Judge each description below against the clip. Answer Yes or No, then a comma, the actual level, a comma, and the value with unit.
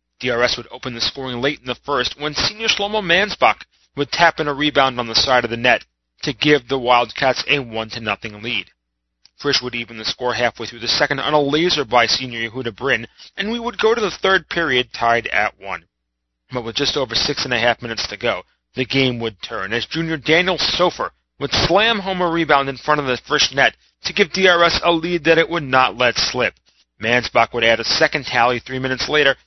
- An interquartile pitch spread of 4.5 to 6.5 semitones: Yes, average, 5.1 semitones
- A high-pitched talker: No, low, 130 Hz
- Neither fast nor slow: No, fast, 220 wpm